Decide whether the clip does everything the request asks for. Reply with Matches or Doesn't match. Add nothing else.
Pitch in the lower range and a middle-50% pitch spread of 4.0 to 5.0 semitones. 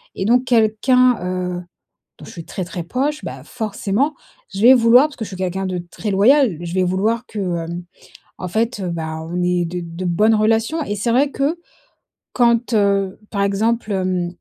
Doesn't match